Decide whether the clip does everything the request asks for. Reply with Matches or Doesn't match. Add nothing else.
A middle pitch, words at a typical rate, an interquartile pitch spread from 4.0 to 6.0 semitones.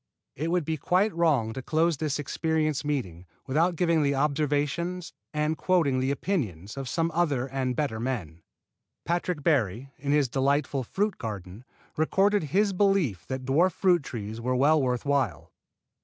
Matches